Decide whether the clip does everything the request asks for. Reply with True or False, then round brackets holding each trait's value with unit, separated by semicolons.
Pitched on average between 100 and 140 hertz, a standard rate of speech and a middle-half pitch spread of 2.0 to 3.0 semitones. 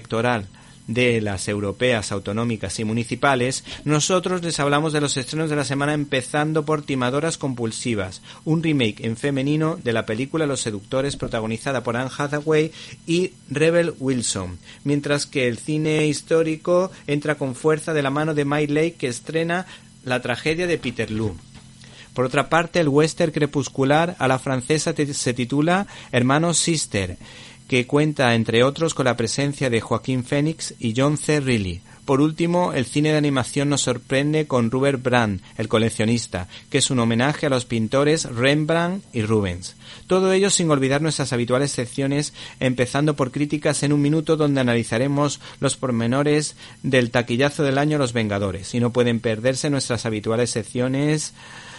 False (135 Hz; 160 wpm; 4.1 semitones)